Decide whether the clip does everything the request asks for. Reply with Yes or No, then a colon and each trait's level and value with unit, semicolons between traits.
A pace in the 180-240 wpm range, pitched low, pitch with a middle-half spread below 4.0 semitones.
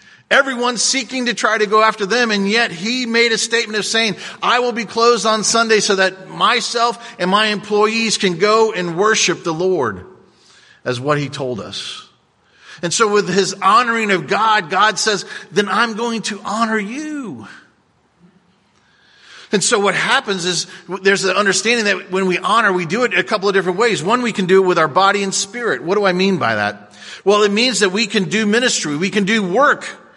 No: fast, 205 wpm; high, 210 Hz; average, 3.4 semitones